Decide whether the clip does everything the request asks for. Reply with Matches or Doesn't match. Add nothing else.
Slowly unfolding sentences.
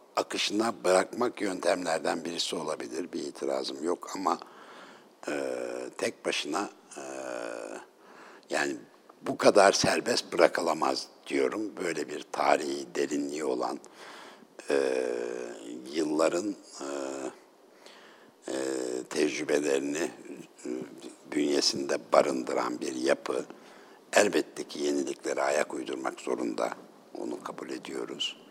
Matches